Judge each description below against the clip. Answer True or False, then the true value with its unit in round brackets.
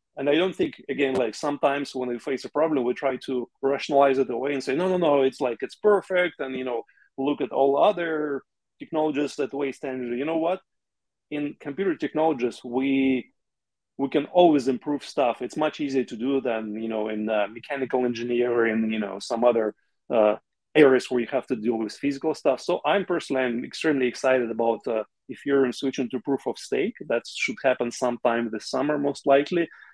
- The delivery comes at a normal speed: False (200 wpm)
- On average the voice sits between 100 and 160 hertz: True (135 Hz)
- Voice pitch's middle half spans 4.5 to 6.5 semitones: False (3.2 semitones)